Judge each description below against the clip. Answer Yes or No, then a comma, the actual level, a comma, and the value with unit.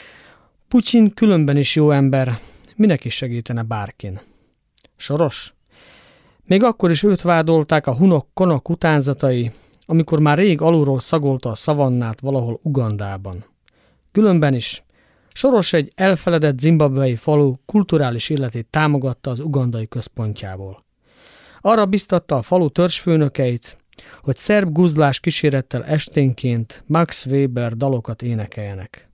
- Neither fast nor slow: Yes, average, 115 wpm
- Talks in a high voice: No, medium, 140 Hz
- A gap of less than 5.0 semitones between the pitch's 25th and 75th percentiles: No, wide, 5.5 semitones